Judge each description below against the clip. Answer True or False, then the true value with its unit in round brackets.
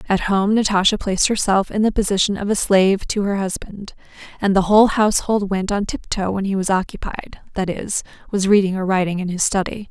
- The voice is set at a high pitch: True (195 Hz)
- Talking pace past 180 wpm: True (200 wpm)